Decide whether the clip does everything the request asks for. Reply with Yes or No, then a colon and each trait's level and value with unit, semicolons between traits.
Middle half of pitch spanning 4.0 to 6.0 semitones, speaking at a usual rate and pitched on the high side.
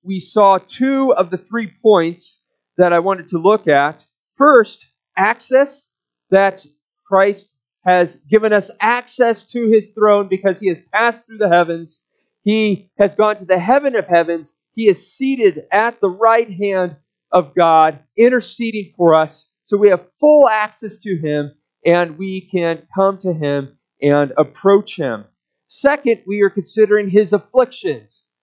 Yes: average, 4.3 semitones; average, 155 wpm; high, 195 Hz